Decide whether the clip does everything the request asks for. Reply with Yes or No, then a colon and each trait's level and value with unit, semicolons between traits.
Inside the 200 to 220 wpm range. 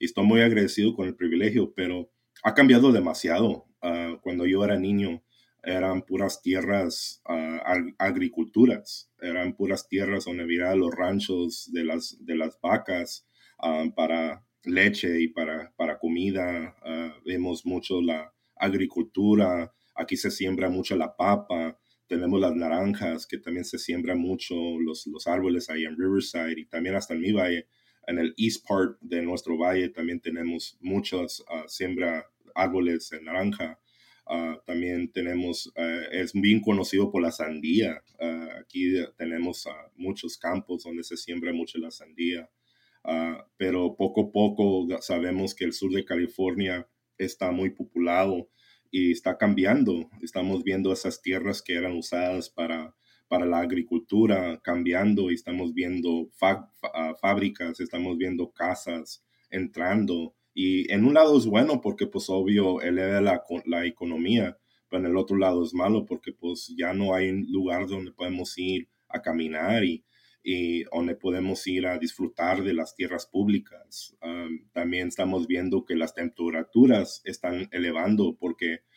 No: average, 150 wpm